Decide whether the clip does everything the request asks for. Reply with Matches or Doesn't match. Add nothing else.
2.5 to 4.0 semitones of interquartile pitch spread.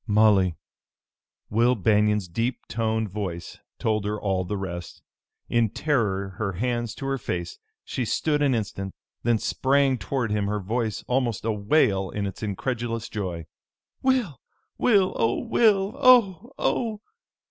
Doesn't match